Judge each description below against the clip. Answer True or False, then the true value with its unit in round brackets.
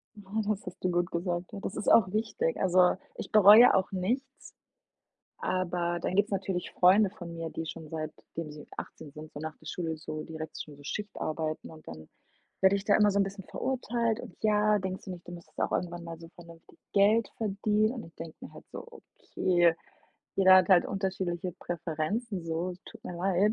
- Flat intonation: False (3.5 semitones)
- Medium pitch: True (180 Hz)